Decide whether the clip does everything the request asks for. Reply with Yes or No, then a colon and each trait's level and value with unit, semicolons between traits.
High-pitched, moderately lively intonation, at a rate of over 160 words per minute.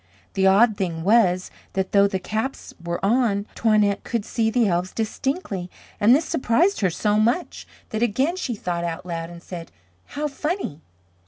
Yes: high, 210 Hz; average, 4.7 semitones; average, 170 wpm